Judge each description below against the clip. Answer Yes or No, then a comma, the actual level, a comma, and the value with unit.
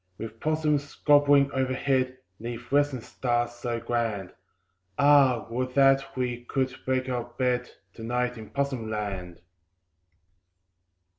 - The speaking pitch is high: No, low, 125 Hz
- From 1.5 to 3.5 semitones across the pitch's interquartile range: Yes, narrow, 2.5 semitones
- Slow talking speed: Yes, slow, 120 wpm